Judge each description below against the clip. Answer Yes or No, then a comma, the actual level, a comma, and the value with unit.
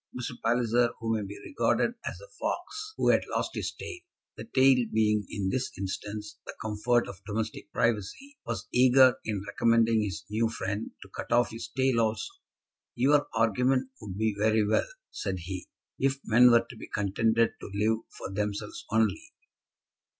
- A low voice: Yes, low, 115 Hz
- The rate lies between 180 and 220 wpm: No, average, 170 wpm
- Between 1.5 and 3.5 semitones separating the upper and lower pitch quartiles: Yes, average, 2.9 semitones